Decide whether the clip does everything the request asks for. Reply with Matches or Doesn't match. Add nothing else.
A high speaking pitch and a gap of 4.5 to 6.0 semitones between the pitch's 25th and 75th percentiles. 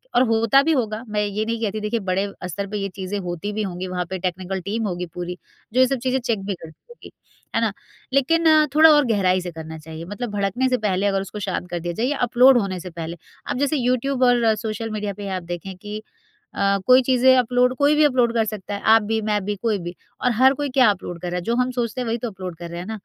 Matches